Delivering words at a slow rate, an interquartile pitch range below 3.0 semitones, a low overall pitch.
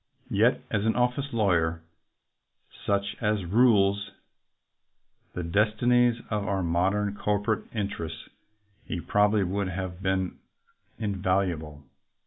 Yes: slow, 115 wpm; narrow, 2.6 semitones; low, 100 Hz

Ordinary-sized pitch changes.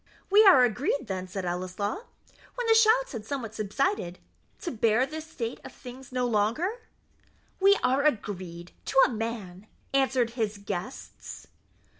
No: wide, 6.7 semitones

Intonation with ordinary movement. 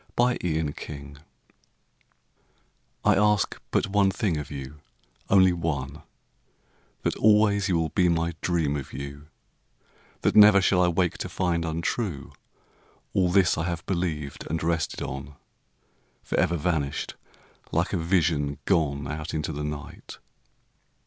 Yes: average, 3.9 semitones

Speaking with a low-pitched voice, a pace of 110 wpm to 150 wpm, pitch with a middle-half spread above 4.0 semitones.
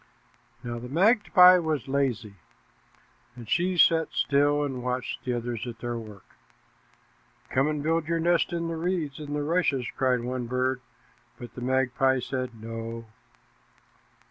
Yes: low, 130 Hz; average, 145 wpm; average, 4.8 semitones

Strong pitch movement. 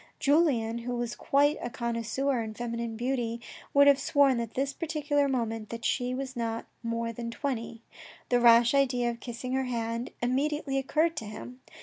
No: average, 2.9 semitones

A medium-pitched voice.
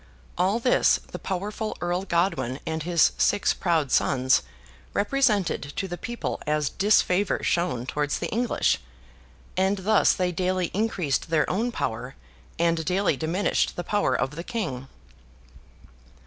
Yes: medium, 180 Hz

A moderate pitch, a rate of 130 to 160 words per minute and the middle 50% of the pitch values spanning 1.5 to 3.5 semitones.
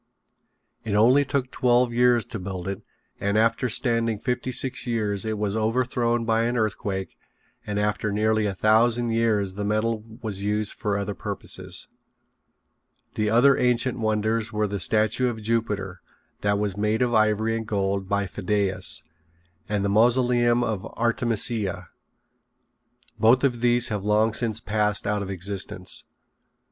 No: low, 110 Hz; average, 150 wpm; narrow, 2.5 semitones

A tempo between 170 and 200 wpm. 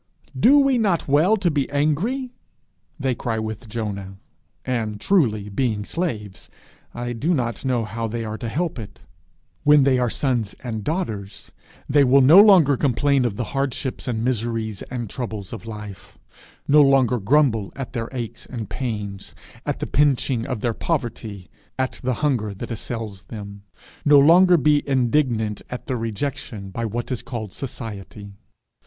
No: average, 160 wpm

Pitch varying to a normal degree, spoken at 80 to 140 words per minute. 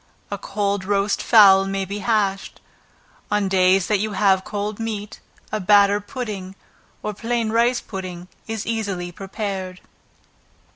No: narrow, 1.9 semitones; slow, 135 wpm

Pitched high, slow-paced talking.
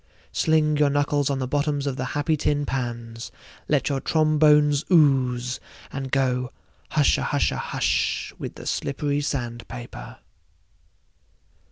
No: medium, 140 Hz; slow, 125 wpm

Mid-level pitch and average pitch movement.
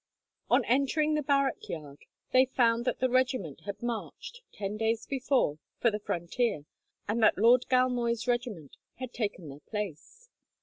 No: high, 235 Hz; average, 4.0 semitones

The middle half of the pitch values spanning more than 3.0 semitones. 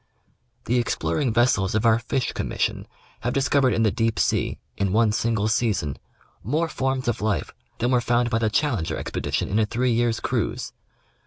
No: narrow, 2.4 semitones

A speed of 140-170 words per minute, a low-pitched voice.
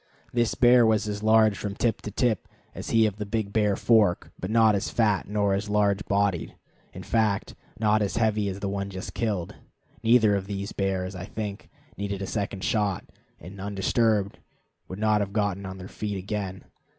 No: average, 190 wpm; low, 100 Hz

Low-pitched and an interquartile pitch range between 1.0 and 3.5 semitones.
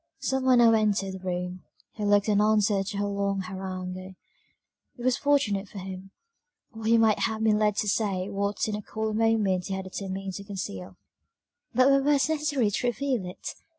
No: high, 205 Hz; average, 2.7 semitones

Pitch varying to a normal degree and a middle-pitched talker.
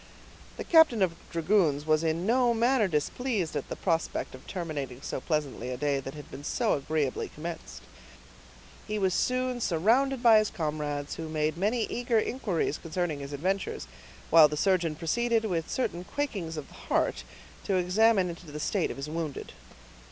No: wide, 6.2 semitones; medium, 170 Hz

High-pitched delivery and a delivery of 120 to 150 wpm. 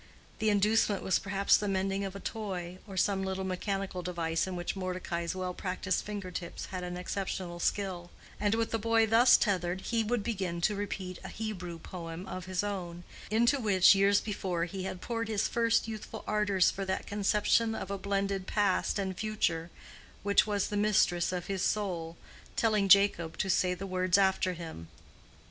No: high, 195 Hz; average, 180 wpm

